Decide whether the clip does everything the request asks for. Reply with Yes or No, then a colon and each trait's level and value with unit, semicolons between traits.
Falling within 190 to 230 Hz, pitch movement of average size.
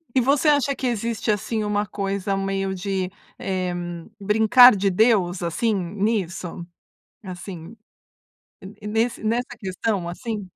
Yes: high, 205 Hz; average, 3.1 semitones